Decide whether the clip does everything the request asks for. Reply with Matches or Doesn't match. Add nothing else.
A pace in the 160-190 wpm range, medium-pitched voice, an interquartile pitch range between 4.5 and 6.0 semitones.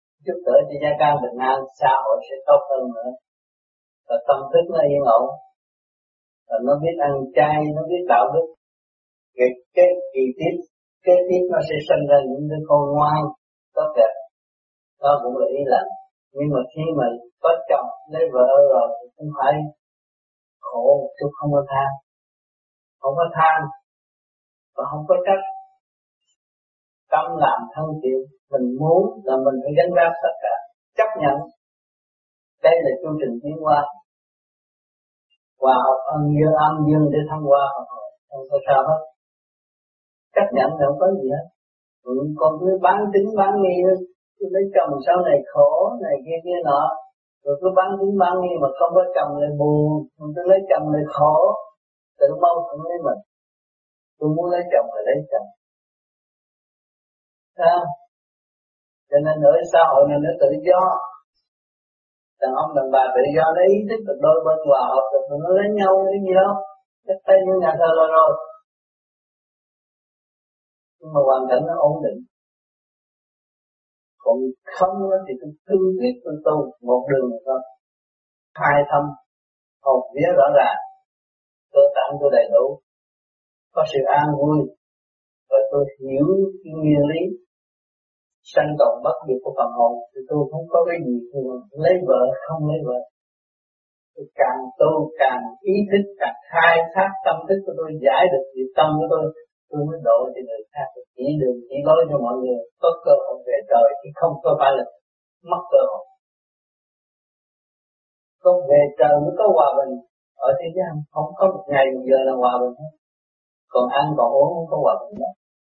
Matches